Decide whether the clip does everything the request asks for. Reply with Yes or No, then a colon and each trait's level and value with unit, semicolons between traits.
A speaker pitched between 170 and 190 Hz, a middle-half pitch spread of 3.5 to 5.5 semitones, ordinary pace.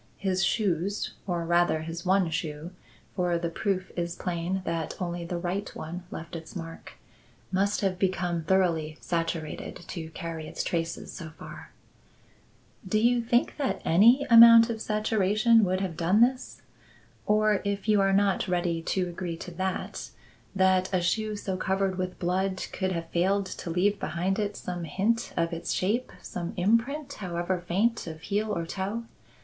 No: medium, 185 Hz; average, 3.0 semitones; average, 165 wpm